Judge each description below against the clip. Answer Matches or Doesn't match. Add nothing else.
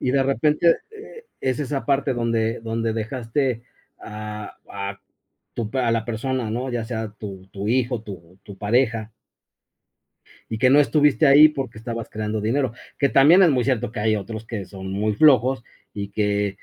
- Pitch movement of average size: Matches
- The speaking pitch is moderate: Doesn't match